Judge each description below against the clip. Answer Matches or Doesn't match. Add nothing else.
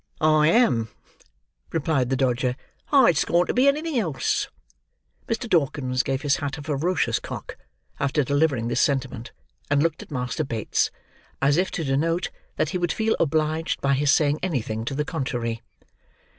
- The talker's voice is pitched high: Doesn't match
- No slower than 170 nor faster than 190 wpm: Doesn't match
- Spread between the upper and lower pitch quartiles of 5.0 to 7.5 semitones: Doesn't match